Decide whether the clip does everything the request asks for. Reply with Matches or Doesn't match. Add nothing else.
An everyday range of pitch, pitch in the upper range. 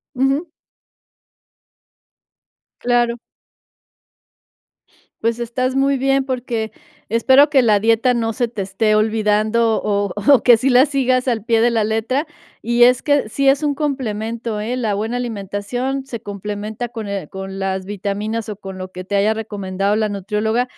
Matches